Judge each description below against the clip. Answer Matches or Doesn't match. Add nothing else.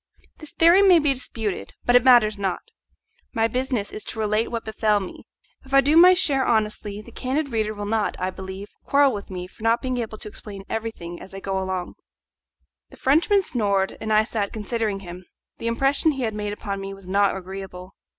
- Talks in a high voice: Matches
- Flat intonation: Doesn't match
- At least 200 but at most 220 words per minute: Matches